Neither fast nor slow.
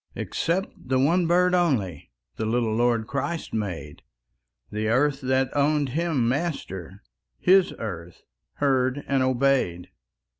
No: slow, 120 wpm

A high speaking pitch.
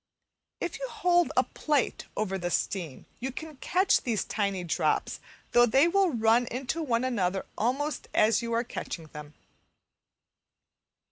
Yes: high, 235 Hz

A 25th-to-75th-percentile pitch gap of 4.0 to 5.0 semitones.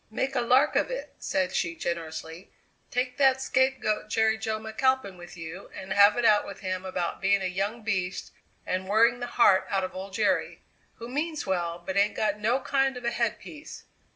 Yes: average, 4.7 semitones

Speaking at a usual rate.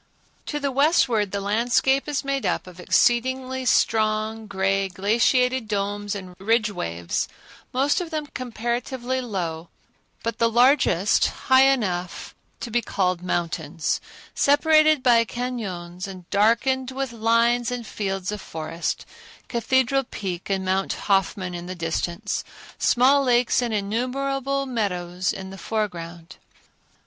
No: slow, 130 wpm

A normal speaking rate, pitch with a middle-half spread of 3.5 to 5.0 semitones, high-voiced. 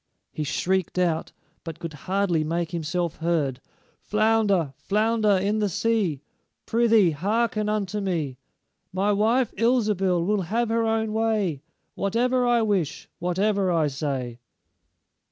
No: slow, 125 wpm; average, 4.7 semitones; high, 195 Hz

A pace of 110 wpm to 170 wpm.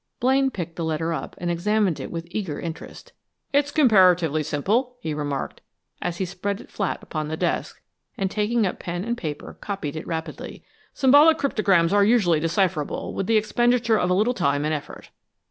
No: average, 180 wpm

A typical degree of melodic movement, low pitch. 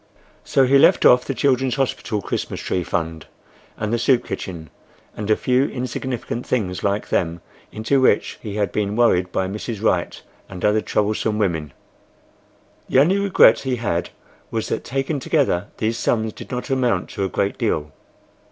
Yes: average, 4.9 semitones; low, 110 Hz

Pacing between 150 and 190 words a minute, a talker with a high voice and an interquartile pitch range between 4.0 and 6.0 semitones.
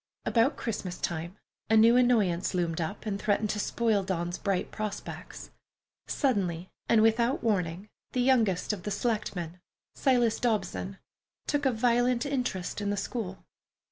No: average, 140 wpm; high, 210 Hz; average, 4.3 semitones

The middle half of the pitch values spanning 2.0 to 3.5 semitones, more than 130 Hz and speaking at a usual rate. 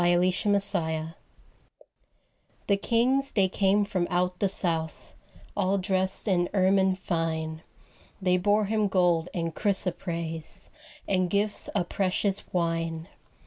No: average, 2.9 semitones; medium, 185 Hz; slow, 115 wpm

